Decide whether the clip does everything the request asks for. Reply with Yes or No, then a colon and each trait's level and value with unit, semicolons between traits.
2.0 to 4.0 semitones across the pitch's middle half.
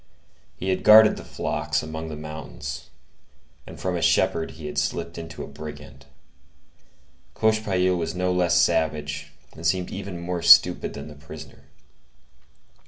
Yes: average, 3.1 semitones